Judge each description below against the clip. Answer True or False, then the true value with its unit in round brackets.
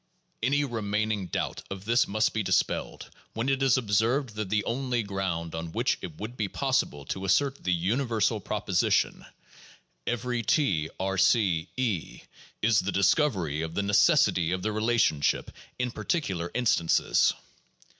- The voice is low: True (105 Hz)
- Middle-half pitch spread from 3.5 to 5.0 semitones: True (4.6 semitones)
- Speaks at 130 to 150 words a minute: True (145 wpm)